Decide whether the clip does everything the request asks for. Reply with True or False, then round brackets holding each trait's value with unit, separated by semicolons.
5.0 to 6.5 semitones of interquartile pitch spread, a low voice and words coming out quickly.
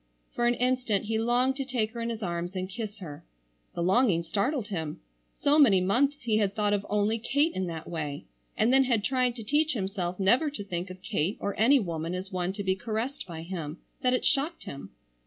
False (5.3 semitones; 210 Hz; 220 wpm)